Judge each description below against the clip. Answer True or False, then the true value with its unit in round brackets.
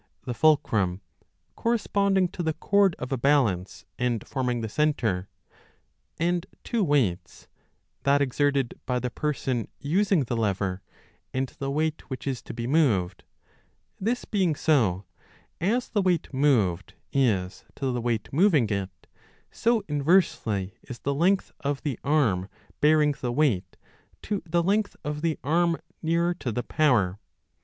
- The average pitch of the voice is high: False (140 Hz)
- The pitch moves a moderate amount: False (6.4 semitones)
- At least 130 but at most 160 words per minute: True (150 wpm)